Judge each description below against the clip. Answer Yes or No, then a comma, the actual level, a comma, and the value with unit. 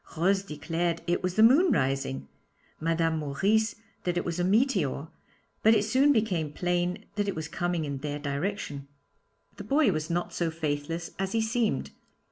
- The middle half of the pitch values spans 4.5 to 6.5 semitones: Yes, average, 5.1 semitones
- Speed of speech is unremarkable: Yes, average, 170 wpm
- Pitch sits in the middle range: Yes, medium, 175 Hz